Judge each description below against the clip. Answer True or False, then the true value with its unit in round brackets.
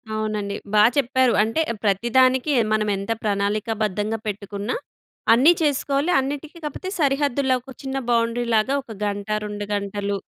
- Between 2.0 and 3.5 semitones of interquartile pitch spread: False (4.6 semitones)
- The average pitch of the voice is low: False (230 Hz)